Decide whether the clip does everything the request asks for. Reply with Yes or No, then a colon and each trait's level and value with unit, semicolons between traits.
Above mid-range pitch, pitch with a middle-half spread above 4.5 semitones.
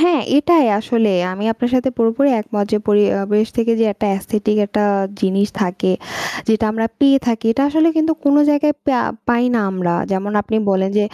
Yes: high, 225 Hz; average, 5.1 semitones